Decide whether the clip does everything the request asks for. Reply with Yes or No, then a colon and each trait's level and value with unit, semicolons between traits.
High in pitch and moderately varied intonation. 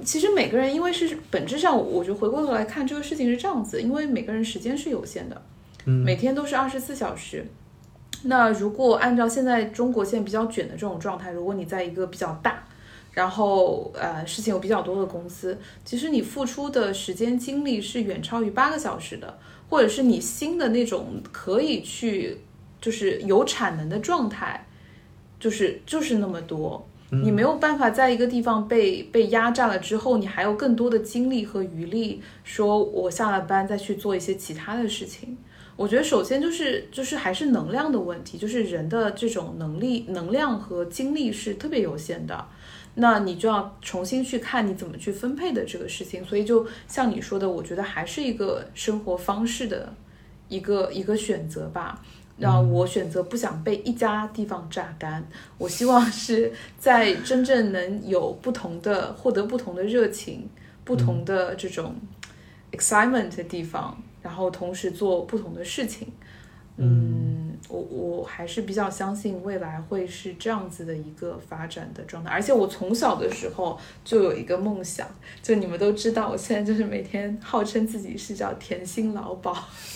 Yes: high, 210 Hz; average, 4.7 semitones